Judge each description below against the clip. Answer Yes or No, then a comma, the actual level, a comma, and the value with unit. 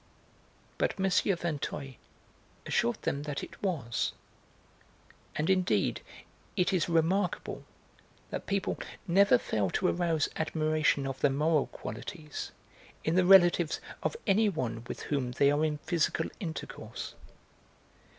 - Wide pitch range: No, average, 4.2 semitones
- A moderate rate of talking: No, slow, 120 wpm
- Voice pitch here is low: No, medium, 160 Hz